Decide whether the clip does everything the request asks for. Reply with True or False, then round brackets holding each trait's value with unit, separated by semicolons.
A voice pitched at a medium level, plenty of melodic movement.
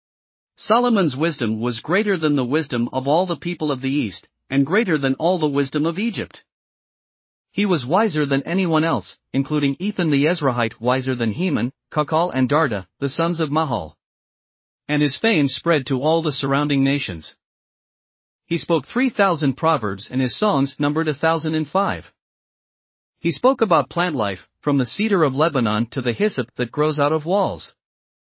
False (150 Hz; 4.1 semitones)